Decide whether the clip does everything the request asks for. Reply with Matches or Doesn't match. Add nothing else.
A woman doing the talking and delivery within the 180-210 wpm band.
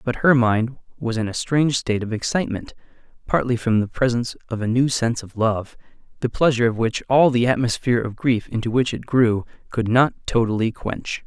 Doesn't match